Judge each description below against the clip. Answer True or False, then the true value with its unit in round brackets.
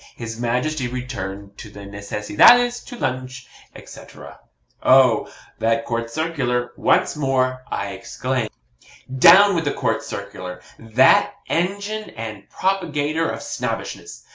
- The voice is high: False (130 Hz)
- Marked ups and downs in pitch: True (5.7 semitones)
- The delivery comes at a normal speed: False (125 wpm)